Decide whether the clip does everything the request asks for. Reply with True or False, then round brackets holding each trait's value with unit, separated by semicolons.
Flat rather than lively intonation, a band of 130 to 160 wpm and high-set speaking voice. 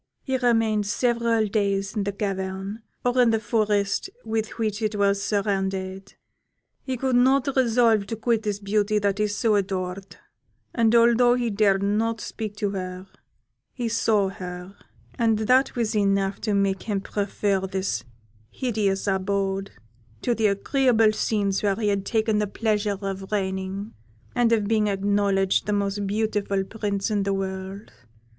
True (2.3 semitones; 150 wpm; 205 Hz)